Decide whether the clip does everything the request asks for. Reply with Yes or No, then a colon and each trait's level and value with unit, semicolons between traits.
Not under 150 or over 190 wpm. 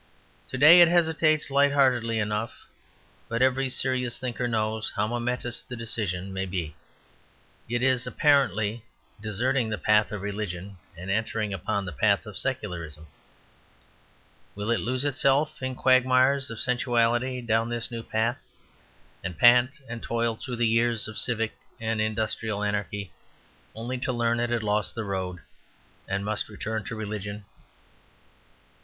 No: average, 140 wpm